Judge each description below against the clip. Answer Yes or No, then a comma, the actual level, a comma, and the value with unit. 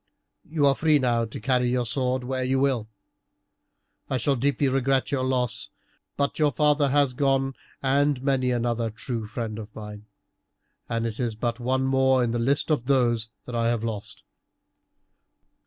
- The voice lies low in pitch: Yes, low, 125 Hz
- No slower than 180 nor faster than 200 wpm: No, average, 165 wpm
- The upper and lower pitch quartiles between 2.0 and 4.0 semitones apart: Yes, average, 2.7 semitones